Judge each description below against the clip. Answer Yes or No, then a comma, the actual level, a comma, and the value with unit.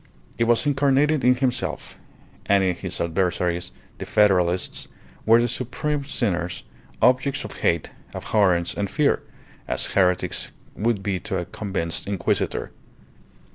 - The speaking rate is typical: No, slow, 125 wpm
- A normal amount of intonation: No, wide, 5.9 semitones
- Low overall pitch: Yes, low, 100 Hz